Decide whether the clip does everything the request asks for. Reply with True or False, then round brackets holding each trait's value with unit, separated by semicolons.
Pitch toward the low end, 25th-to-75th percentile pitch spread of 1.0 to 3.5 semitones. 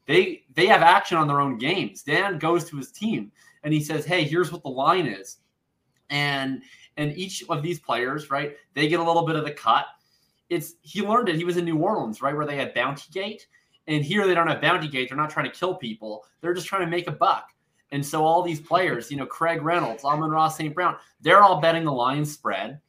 False (160 Hz; 3.2 semitones)